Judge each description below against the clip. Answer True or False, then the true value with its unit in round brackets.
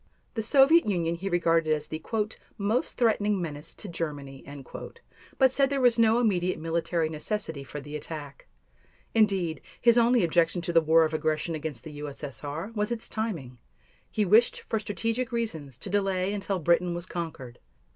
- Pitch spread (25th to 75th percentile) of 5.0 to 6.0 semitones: True (5.6 semitones)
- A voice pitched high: False (175 Hz)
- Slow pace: False (165 wpm)